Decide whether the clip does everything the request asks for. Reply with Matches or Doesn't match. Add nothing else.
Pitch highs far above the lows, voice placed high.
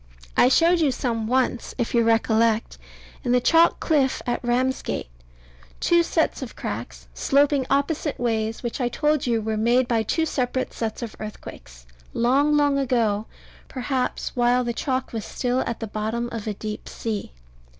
Doesn't match